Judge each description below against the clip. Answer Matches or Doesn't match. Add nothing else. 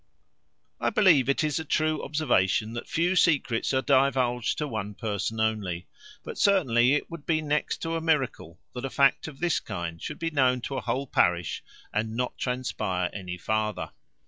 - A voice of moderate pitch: Doesn't match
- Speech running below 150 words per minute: Doesn't match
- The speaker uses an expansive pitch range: Matches